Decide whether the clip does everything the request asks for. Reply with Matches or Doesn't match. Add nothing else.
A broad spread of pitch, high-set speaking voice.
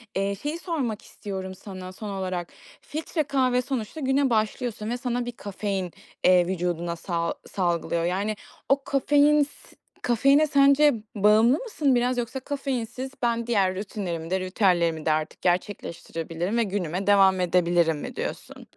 Matches